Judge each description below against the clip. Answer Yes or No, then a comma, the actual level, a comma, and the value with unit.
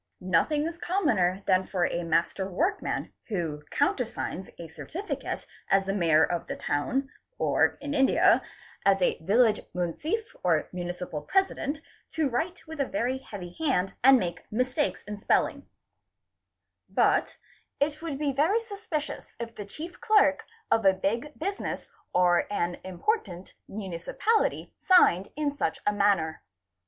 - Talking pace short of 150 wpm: Yes, average, 140 wpm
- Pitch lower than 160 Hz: No, high, 225 Hz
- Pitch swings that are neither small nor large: No, wide, 9.0 semitones